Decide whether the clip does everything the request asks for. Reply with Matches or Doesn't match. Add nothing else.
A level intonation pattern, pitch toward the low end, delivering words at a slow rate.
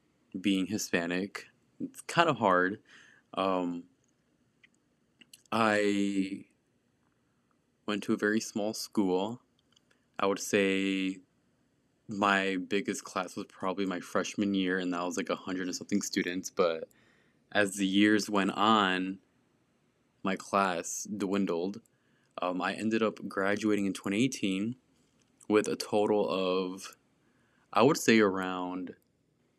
Matches